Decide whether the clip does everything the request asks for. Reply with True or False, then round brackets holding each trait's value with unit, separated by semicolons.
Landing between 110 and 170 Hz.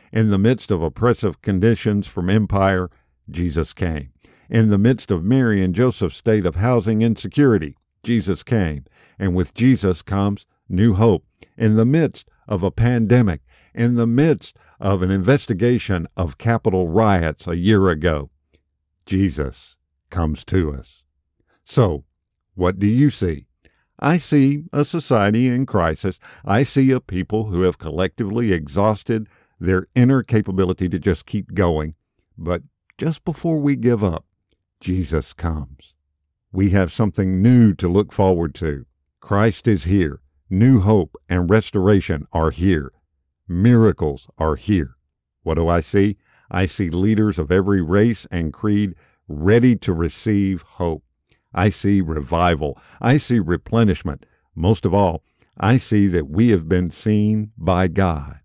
False (95 Hz)